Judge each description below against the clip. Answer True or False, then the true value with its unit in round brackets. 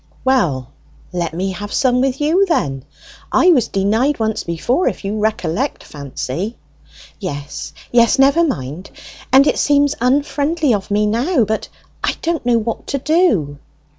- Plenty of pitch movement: True (7.5 semitones)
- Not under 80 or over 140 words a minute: False (150 wpm)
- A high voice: True (230 Hz)